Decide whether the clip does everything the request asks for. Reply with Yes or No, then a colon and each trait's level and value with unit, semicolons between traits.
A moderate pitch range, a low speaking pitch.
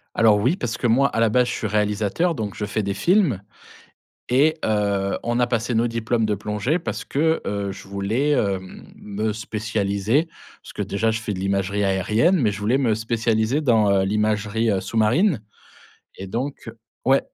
Yes: average, 3.1 semitones; low, 110 Hz